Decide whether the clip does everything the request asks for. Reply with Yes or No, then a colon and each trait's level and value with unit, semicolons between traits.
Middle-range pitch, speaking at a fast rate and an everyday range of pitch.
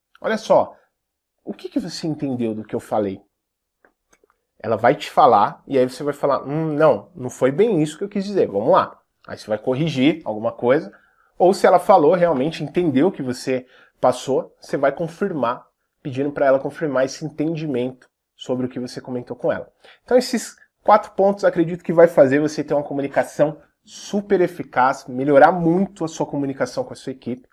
Yes: medium, 145 Hz; fast, 190 wpm; average, 4.9 semitones